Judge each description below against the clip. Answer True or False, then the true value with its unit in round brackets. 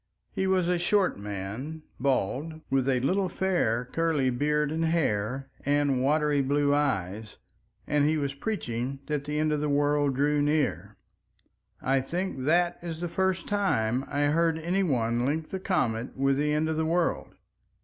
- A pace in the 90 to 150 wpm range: False (170 wpm)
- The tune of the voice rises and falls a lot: False (3.7 semitones)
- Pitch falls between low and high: True (145 Hz)